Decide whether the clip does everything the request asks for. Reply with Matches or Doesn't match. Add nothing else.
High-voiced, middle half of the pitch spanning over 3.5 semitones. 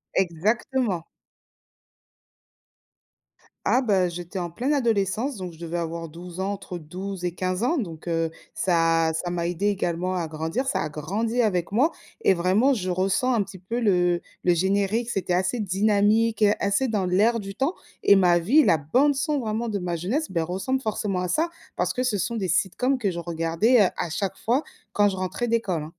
Matches